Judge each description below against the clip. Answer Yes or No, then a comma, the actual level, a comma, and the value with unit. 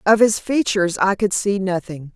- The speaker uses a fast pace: No, average, 195 wpm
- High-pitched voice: Yes, high, 195 Hz